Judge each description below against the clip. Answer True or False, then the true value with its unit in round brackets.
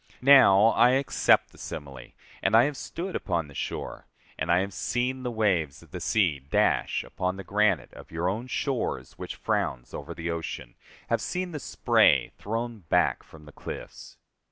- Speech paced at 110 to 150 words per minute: False (180 wpm)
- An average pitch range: False (7.0 semitones)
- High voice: False (100 Hz)